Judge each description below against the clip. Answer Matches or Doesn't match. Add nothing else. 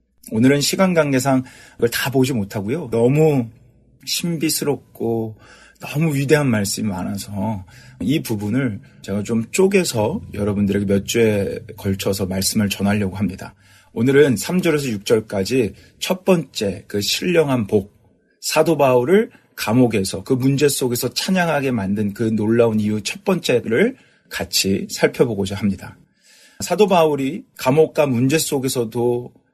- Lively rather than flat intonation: Matches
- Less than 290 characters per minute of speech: Matches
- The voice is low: Matches